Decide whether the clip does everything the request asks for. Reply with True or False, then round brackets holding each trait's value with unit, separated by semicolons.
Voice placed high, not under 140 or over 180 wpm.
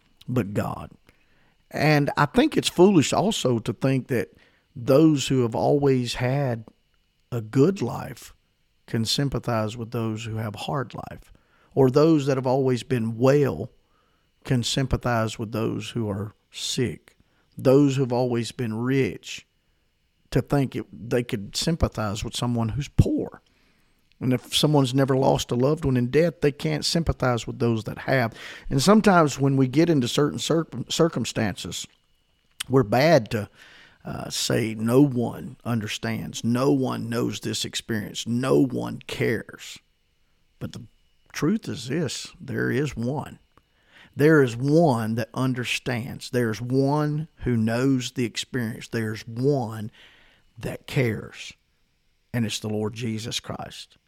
False (125 Hz; 145 wpm)